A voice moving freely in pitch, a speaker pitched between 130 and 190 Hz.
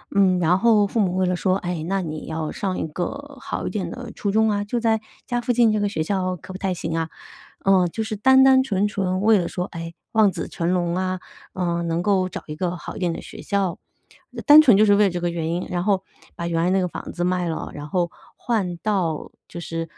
No: average, 3.3 semitones; medium, 185 Hz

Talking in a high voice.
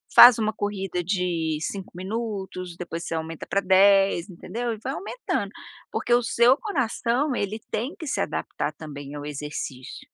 Yes: high, 195 Hz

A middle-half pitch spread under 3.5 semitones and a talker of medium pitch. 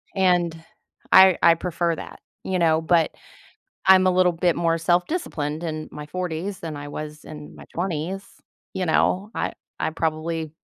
Yes: narrow, 2.5 semitones; medium, 170 Hz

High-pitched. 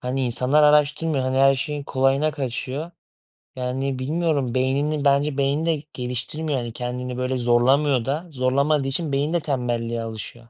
No: low, 135 Hz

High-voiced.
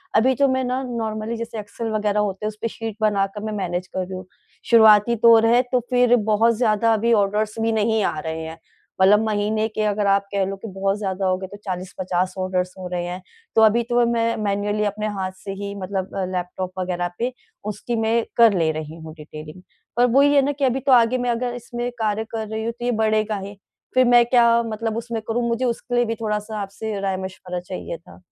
Yes: high, 215 Hz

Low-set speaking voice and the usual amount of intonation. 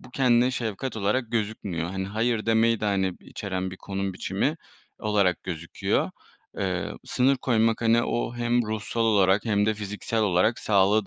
Yes: low, 105 Hz; average, 3.1 semitones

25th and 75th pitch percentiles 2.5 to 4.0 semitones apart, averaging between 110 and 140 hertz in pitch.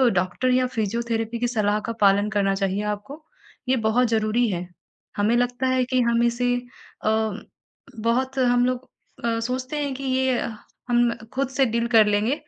No: average, 3.0 semitones; high, 235 Hz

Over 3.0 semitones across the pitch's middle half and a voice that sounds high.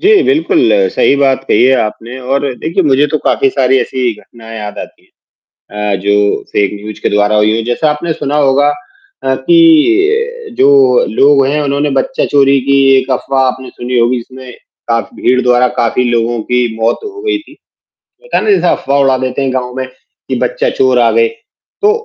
No: average, 3.7 semitones; low, 130 Hz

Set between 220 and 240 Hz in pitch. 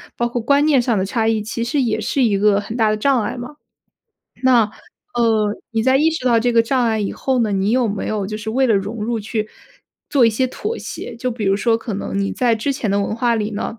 Yes: high, 230 Hz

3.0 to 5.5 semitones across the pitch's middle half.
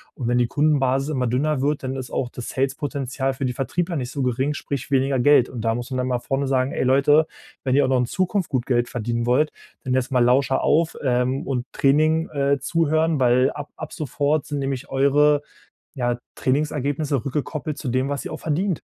No: narrow, 2.5 semitones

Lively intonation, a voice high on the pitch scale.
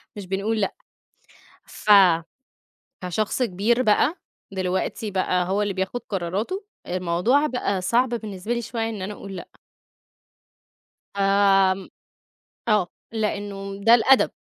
No: average, 3.2 semitones; high, 200 Hz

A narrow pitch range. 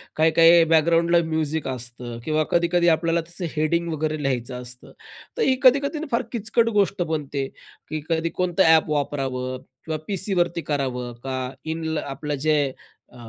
No: average, 3.7 semitones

